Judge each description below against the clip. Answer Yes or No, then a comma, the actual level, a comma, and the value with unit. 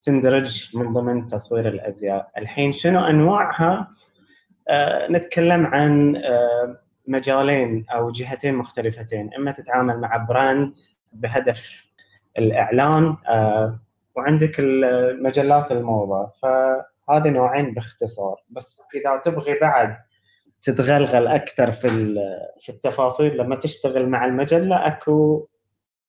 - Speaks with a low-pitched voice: Yes, low, 130 Hz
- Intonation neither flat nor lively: Yes, average, 3.8 semitones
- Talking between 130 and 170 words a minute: No, average, 95 wpm